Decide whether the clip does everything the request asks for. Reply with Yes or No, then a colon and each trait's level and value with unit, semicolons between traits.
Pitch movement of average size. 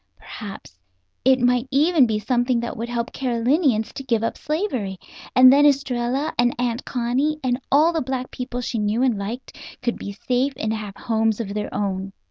Yes: average, 3.1 semitones